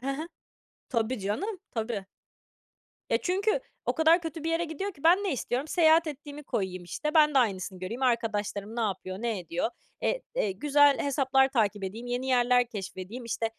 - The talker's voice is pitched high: Yes, very high, 250 Hz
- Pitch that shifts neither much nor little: No, wide, 6.4 semitones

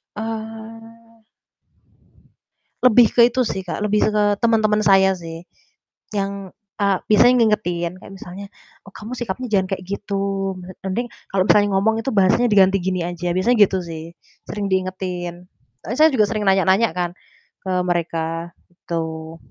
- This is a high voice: Yes, high, 195 Hz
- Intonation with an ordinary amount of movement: Yes, average, 3.3 semitones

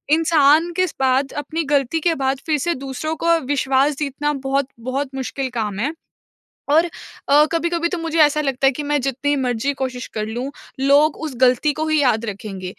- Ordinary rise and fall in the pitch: Yes, average, 3.0 semitones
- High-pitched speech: Yes, very high, 280 Hz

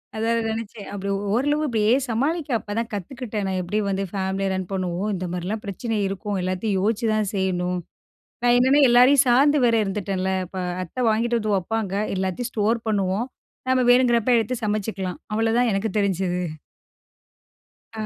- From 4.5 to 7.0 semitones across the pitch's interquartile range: No, average, 3.7 semitones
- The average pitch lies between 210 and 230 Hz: Yes, high, 215 Hz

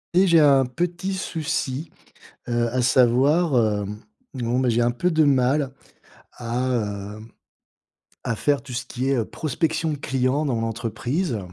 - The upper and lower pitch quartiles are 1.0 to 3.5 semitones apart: No, average, 4.1 semitones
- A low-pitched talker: Yes, low, 130 Hz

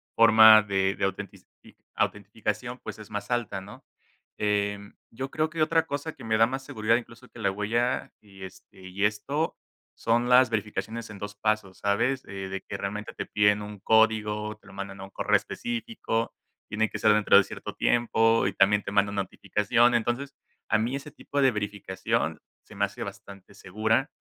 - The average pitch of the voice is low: Yes, low, 105 Hz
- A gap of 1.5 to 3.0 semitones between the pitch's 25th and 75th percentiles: Yes, average, 2.7 semitones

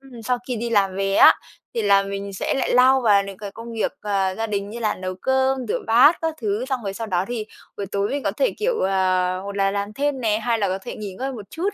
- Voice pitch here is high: Yes, high, 215 Hz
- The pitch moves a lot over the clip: No, average, 4.1 semitones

